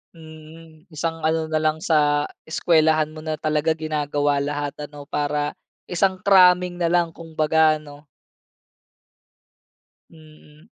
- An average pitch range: No, narrow, 1.6 semitones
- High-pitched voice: No, medium, 155 Hz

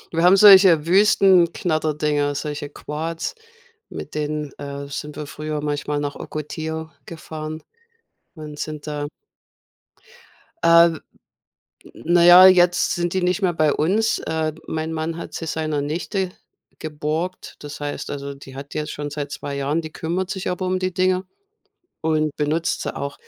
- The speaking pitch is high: No, medium, 155 Hz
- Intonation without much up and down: No, average, 3.0 semitones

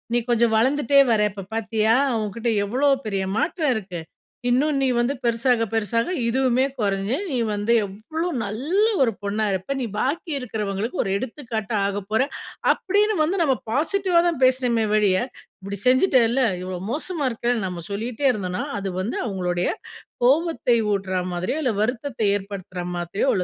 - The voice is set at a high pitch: Yes, high, 230 Hz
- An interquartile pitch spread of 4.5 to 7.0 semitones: Yes, average, 5.0 semitones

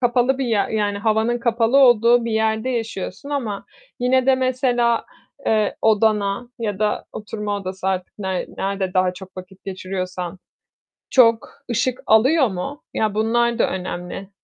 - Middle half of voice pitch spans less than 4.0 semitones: Yes, average, 3.6 semitones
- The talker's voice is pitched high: Yes, high, 220 Hz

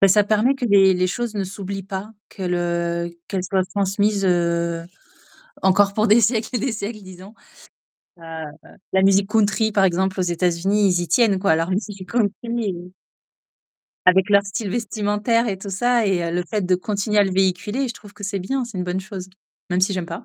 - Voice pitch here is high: Yes, high, 195 Hz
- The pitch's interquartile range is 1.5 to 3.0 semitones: Yes, narrow, 2.4 semitones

